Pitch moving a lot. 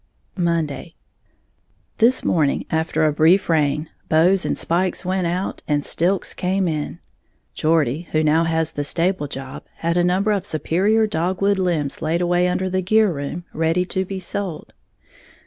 No: average, 3.0 semitones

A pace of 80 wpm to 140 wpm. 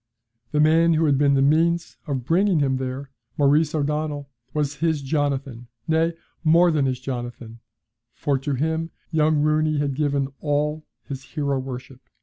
No: average, 155 wpm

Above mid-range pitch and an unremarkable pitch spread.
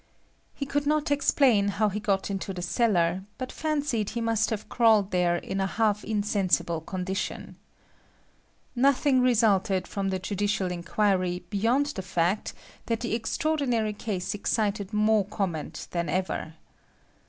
Yes: high, 205 Hz; average, 3.5 semitones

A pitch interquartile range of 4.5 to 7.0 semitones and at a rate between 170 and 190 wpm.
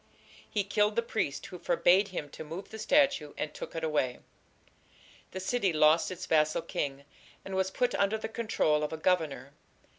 Yes: average, 5.3 semitones; average, 180 wpm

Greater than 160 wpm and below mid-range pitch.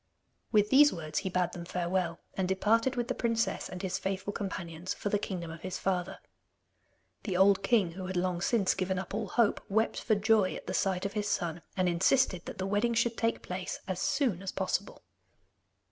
No: fast, 205 wpm; high, 190 Hz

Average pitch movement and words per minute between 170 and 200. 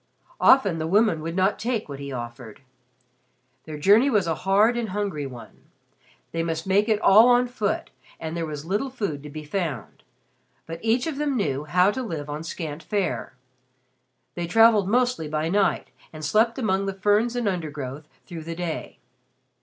No: wide, 5.9 semitones; average, 175 wpm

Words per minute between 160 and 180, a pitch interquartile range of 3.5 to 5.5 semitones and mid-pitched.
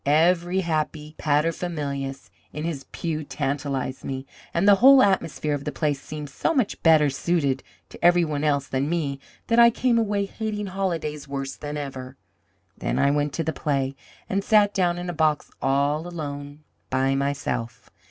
Yes: average, 170 wpm; average, 4.0 semitones; medium, 150 Hz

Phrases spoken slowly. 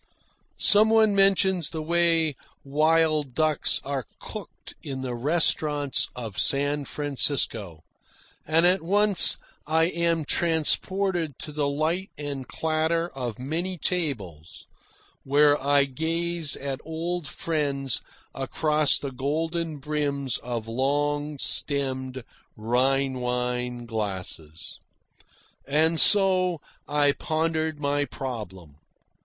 Yes: slow, 105 wpm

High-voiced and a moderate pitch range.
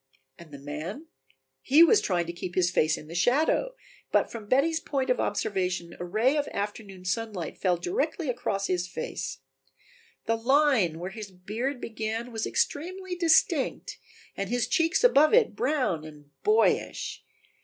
No: high, 220 Hz; wide, 8.3 semitones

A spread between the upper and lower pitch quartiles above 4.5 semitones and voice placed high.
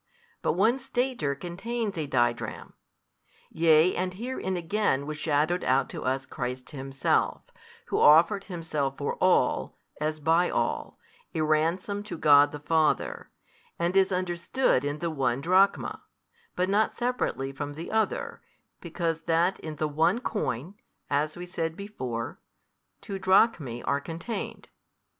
No: average, 4.9 semitones; medium, 165 Hz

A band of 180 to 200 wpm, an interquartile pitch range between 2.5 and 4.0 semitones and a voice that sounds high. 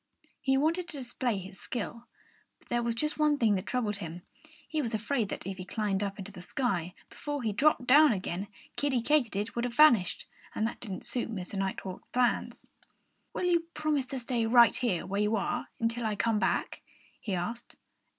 No: average, 190 wpm; average, 5.0 semitones; high, 230 Hz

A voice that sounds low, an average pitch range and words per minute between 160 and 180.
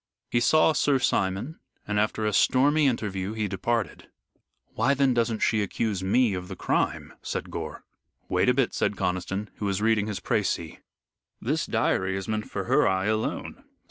Yes: low, 110 Hz; average, 3.9 semitones; average, 175 wpm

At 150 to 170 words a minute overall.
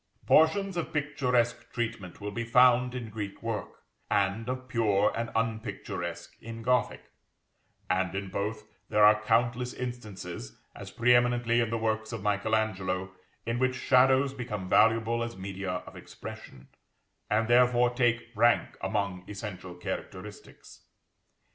No: slow, 135 wpm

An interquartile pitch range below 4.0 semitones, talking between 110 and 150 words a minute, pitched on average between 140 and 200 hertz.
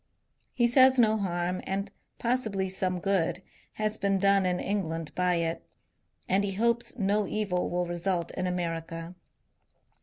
Yes: average, 2.9 semitones; average, 145 wpm; high, 190 Hz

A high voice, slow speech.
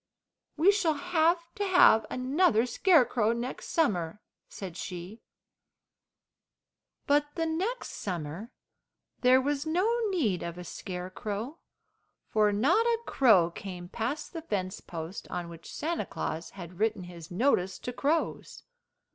Yes: high, 230 Hz; slow, 130 wpm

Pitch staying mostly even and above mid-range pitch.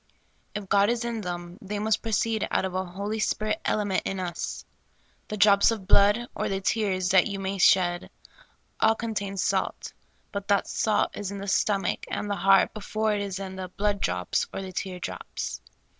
Yes: narrow, 2.0 semitones; high, 200 Hz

